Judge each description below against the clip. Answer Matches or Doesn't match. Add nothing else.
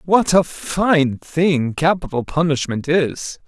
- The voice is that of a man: Matches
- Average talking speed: Doesn't match